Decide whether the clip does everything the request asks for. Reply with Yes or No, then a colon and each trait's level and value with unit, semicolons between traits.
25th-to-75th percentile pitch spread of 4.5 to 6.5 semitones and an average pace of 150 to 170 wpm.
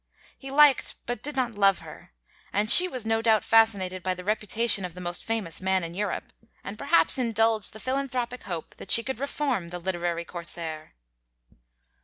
No: average, 5.1 semitones; average, 180 wpm